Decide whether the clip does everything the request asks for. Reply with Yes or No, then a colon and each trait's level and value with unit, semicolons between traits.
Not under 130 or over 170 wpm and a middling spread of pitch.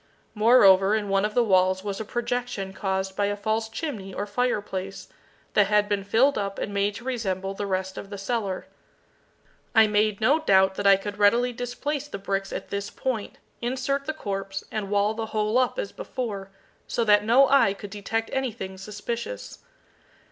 No: average, 185 wpm; average, 3.4 semitones